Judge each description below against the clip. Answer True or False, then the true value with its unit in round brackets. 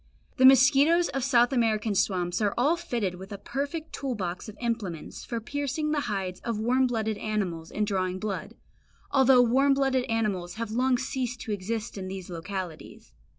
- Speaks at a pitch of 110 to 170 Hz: False (225 Hz)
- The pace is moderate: True (175 wpm)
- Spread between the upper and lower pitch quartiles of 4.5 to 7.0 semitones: True (5.2 semitones)